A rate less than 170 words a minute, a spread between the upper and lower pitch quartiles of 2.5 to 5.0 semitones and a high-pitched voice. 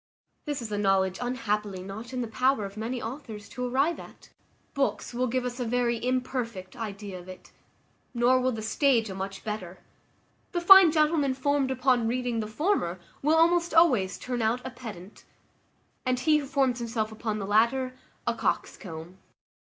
No: average, 175 wpm; average, 3.8 semitones; high, 240 Hz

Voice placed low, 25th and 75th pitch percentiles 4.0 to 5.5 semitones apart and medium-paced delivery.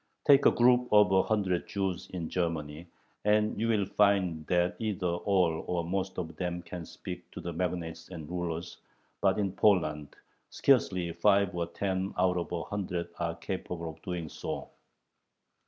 No: very low, 90 Hz; average, 2.8 semitones; average, 165 wpm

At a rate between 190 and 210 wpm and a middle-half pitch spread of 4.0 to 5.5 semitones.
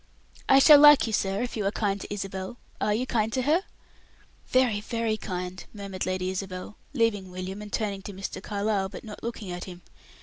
No: average, 200 wpm; average, 3.2 semitones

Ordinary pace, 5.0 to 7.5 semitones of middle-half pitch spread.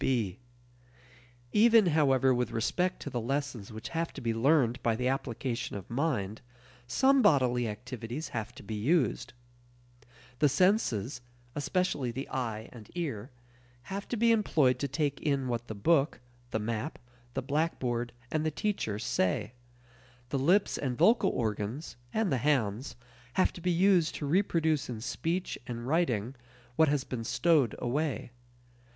Yes: average, 150 wpm; wide, 5.6 semitones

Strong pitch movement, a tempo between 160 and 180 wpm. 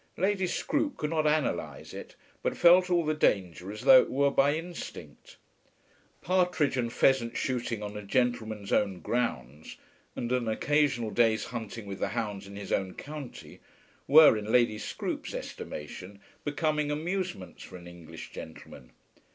No: wide, 6.8 semitones; average, 150 wpm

